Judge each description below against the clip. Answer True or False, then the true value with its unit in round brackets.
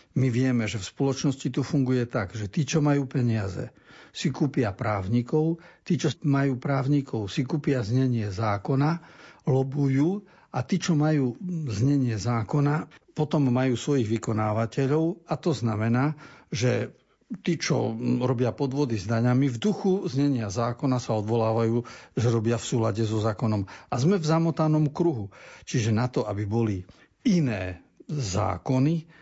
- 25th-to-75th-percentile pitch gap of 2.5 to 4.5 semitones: False (4.9 semitones)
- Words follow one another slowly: False (140 wpm)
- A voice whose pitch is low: True (130 Hz)